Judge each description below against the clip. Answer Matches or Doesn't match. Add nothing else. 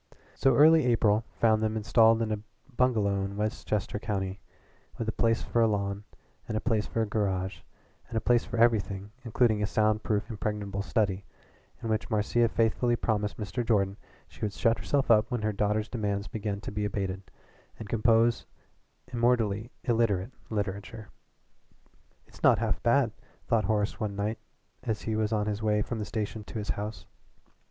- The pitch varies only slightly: Matches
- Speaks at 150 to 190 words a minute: Matches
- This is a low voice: Matches